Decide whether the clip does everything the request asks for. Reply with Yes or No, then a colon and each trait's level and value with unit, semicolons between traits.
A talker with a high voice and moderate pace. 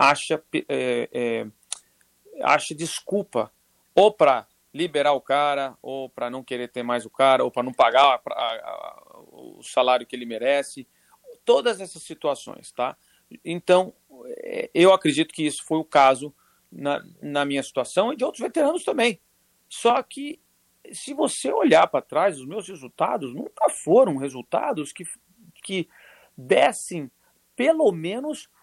No: medium, 160 Hz; average, 145 wpm